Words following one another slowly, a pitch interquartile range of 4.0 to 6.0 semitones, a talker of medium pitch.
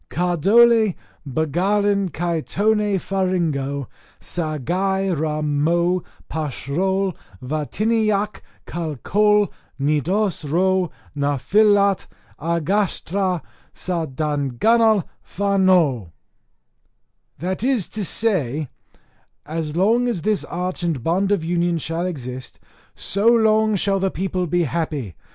Yes: slow, 95 wpm; average, 4.5 semitones; medium, 180 Hz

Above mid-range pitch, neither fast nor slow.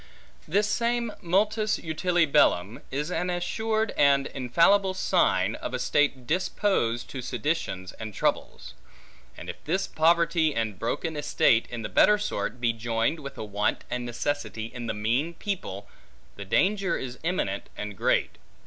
No: medium, 145 Hz; average, 150 wpm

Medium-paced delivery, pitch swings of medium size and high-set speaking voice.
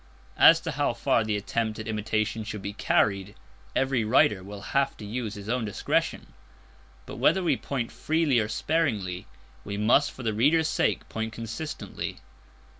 No: average, 165 wpm; average, 4.0 semitones; low, 110 Hz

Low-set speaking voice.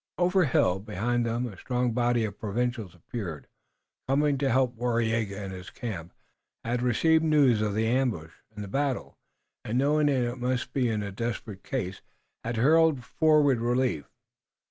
Yes: low, 120 Hz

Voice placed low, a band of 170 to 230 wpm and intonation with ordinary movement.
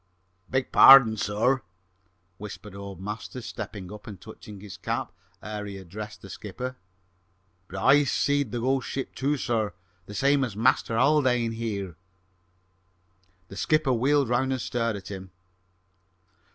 No: low, 115 Hz; average, 140 wpm; average, 4.5 semitones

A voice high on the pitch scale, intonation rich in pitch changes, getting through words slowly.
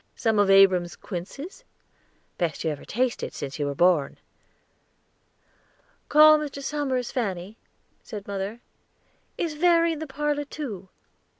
Yes: high, 225 Hz; wide, 8.3 semitones; slow, 125 wpm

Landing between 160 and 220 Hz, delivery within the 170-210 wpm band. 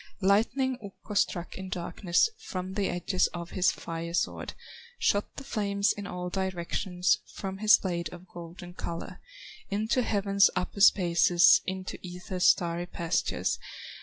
No: medium, 185 Hz; slow, 135 wpm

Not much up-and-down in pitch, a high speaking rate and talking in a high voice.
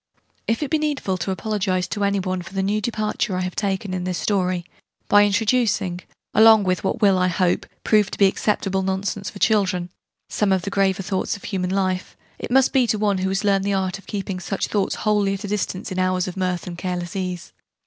Yes: narrow, 2.0 semitones; fast, 225 wpm; high, 195 Hz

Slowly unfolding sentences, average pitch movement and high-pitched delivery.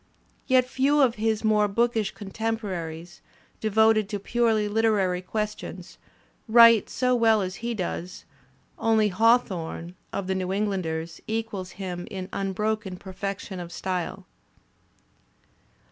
Yes: slow, 120 wpm; average, 3.3 semitones; high, 210 Hz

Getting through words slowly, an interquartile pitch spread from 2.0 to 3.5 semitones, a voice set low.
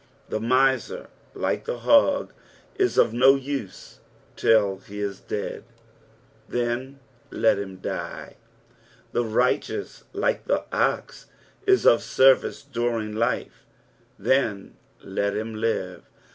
No: slow, 115 wpm; average, 4.2 semitones; low, 120 Hz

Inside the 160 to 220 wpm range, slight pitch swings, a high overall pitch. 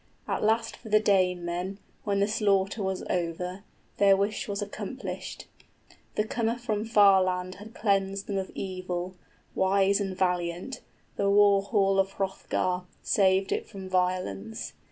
No: average, 150 wpm; narrow, 1.8 semitones; high, 195 Hz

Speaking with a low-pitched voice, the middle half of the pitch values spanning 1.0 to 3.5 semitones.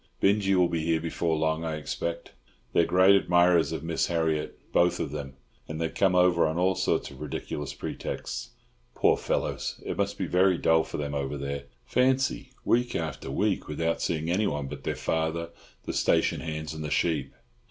Yes: very low, 80 Hz; narrow, 2.6 semitones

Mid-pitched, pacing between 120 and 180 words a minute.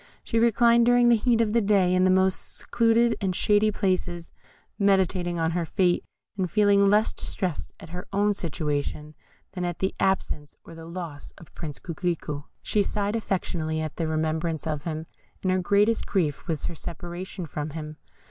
Yes: medium, 180 Hz; average, 175 wpm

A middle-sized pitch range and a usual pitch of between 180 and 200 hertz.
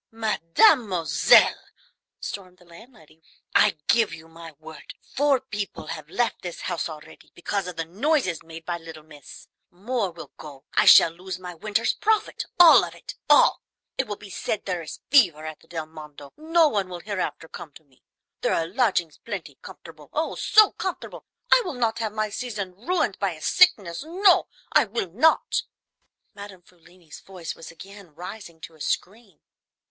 No: wide, 5.8 semitones; medium, 185 Hz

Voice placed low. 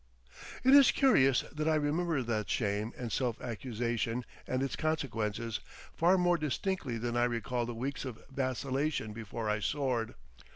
Yes: low, 125 Hz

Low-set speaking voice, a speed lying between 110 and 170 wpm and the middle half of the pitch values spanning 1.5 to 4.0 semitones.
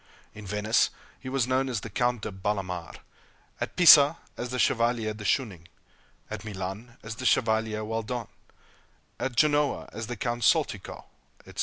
Yes: low, 115 Hz; average, 155 wpm; average, 2.9 semitones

